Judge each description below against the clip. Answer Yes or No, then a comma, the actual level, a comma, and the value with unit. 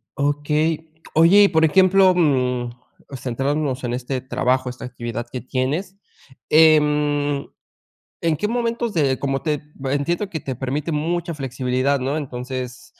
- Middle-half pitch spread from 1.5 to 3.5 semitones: No, average, 3.9 semitones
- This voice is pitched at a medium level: Yes, medium, 145 Hz